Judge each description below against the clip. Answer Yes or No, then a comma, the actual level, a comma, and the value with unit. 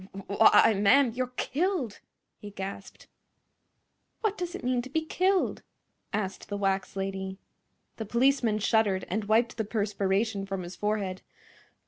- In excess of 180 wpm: No, slow, 135 wpm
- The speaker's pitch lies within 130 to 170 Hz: No, high, 215 Hz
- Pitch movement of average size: Yes, average, 4.4 semitones